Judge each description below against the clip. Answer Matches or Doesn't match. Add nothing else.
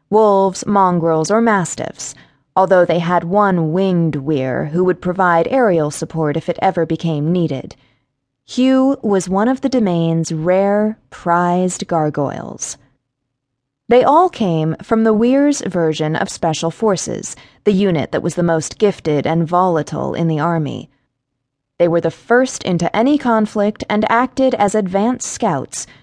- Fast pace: Doesn't match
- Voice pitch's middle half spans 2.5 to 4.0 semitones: Doesn't match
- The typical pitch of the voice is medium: Matches